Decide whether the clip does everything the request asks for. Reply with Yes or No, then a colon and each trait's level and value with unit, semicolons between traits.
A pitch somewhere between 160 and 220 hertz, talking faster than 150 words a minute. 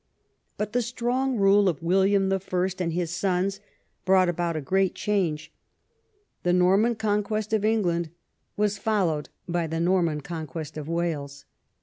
No: medium, 185 Hz; average, 140 wpm